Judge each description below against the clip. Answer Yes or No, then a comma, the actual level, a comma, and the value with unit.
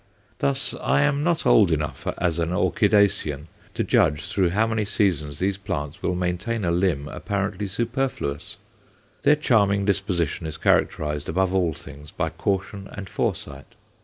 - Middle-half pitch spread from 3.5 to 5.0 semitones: Yes, average, 4.6 semitones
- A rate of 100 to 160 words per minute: Yes, average, 150 wpm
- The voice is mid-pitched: No, very low, 95 Hz